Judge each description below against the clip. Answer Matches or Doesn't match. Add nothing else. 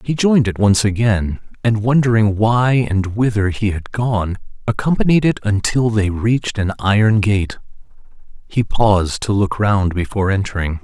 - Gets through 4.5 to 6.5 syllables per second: Matches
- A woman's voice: Doesn't match